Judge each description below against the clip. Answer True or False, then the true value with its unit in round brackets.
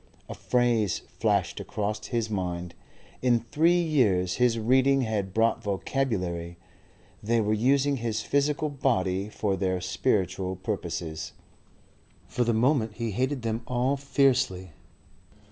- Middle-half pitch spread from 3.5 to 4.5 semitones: False (5.4 semitones)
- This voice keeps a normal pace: False (125 wpm)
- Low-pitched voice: True (110 Hz)